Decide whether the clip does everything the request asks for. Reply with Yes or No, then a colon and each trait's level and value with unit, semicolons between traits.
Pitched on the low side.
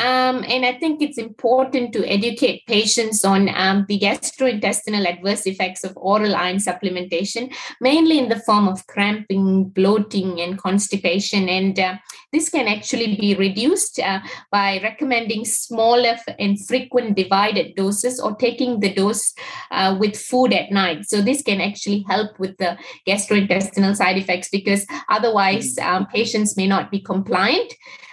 No: high, 205 Hz